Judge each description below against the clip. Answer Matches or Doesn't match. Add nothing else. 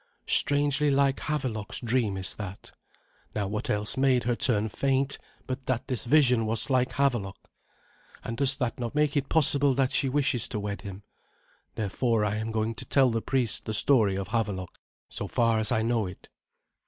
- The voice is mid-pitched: Doesn't match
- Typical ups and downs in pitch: Matches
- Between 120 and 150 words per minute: Doesn't match